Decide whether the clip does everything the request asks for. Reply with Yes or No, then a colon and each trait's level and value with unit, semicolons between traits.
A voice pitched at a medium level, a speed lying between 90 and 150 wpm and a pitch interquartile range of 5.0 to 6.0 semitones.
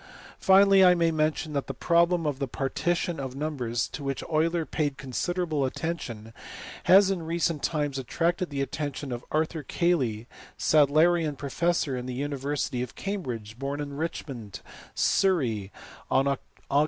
No: medium, 145 Hz; average, 145 wpm; average, 4.1 semitones